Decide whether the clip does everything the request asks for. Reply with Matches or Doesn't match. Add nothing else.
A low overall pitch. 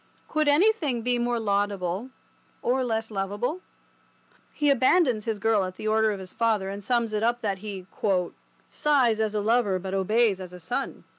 Doesn't match